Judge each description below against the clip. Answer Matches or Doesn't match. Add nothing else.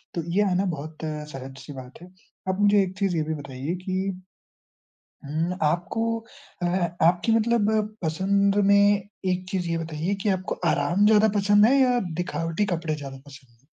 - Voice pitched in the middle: Matches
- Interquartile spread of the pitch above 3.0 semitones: Matches